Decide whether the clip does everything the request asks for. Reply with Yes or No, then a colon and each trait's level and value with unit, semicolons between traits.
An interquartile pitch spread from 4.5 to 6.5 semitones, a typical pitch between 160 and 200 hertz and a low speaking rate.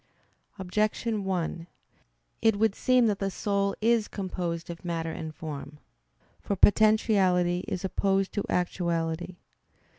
No: average, 3.3 semitones; high, 190 Hz; slow, 120 wpm